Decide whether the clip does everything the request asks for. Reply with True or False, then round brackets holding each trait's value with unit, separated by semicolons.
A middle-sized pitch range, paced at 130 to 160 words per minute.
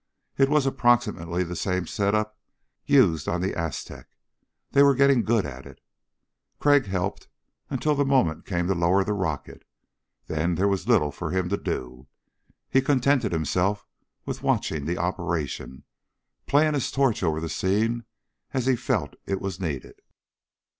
False (6.4 semitones; 155 wpm)